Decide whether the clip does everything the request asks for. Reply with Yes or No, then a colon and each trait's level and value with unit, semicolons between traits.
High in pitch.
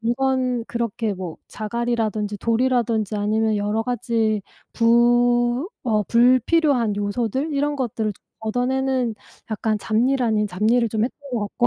Yes: high, 235 Hz